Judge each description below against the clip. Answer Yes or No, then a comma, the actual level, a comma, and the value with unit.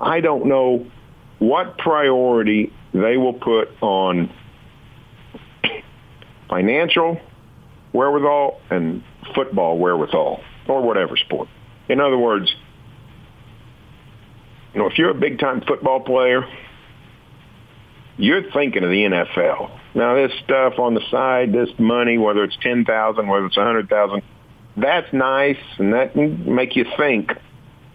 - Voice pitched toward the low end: Yes, low, 120 Hz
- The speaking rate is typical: No, slow, 125 wpm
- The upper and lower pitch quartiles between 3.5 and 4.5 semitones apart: Yes, average, 4.2 semitones